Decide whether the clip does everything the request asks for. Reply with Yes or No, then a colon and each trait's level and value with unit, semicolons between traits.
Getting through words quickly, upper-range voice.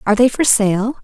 Yes: fast, 235 wpm; high, 230 Hz